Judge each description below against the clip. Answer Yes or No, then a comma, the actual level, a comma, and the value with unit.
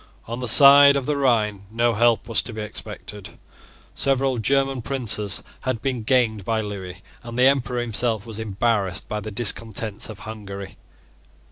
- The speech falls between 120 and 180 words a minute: Yes, average, 160 wpm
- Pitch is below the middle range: Yes, low, 115 Hz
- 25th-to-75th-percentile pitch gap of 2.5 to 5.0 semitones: Yes, average, 3.0 semitones